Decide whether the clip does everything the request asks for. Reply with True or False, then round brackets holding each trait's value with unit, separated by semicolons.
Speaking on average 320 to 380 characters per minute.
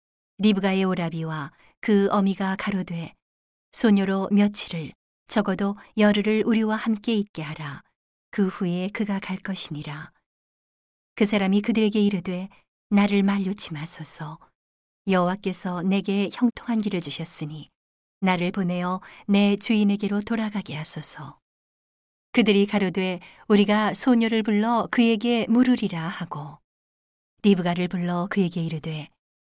False (275 characters per minute)